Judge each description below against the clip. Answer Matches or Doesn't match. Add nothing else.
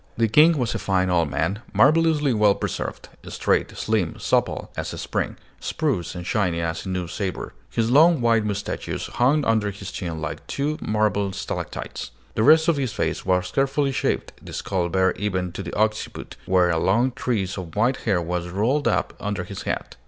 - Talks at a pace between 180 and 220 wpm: Matches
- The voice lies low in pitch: Matches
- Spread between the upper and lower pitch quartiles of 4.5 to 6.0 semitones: Matches